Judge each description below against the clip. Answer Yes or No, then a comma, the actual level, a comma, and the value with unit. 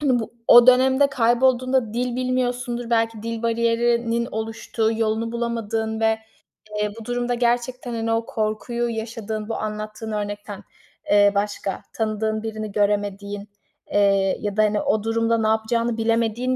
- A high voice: Yes, high, 225 Hz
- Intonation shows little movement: Yes, narrow, 1.8 semitones